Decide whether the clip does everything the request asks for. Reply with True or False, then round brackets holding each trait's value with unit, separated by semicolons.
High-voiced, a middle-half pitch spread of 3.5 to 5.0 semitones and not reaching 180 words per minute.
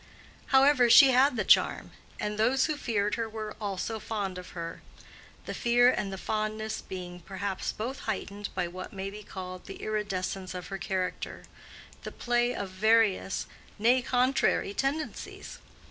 True (210 Hz; 4.0 semitones; 150 wpm)